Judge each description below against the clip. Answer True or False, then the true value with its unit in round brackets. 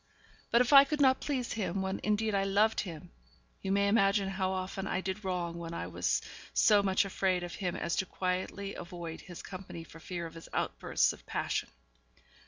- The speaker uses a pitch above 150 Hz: True (190 Hz)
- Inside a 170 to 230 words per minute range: True (195 wpm)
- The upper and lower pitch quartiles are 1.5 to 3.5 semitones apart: True (2.4 semitones)